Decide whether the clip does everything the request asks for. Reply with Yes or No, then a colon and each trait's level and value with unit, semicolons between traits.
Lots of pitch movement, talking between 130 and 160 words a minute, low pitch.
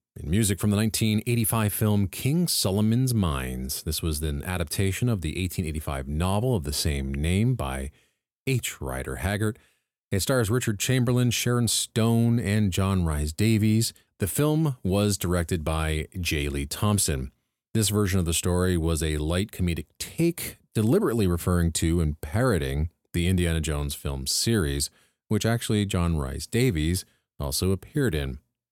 Yes: wide, 6.0 semitones; average, 145 wpm; very low, 95 Hz